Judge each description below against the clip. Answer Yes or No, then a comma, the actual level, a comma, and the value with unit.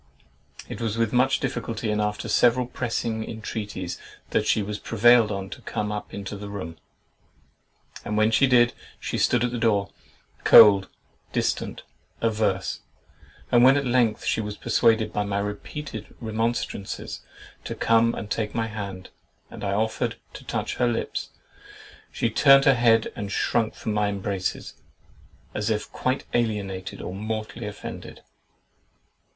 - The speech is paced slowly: No, average, 150 wpm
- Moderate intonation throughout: No, narrow, 2.3 semitones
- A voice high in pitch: No, low, 110 Hz